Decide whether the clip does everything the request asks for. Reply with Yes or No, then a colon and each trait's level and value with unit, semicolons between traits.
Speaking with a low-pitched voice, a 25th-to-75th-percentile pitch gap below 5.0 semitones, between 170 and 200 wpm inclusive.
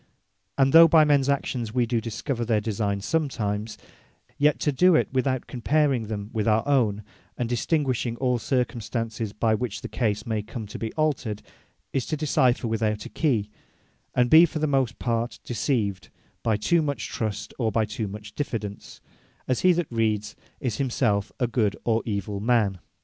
Yes: low, 115 Hz; average, 4.0 semitones; average, 175 wpm